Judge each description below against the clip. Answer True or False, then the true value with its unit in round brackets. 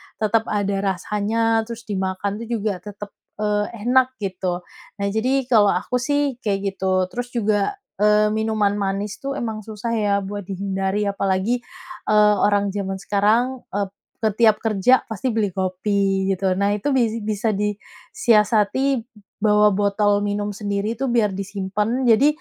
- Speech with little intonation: True (2.1 semitones)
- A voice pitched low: False (210 Hz)